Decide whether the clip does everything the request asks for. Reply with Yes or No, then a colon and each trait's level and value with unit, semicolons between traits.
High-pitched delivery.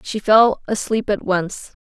Yes: high, 205 Hz